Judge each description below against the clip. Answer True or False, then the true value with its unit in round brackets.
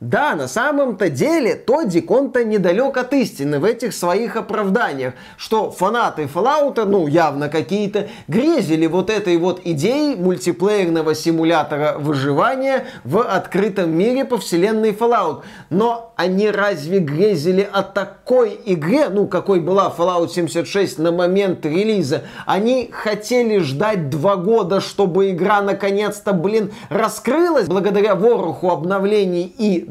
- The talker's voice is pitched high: True (195 Hz)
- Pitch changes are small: False (4.0 semitones)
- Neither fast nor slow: True (125 wpm)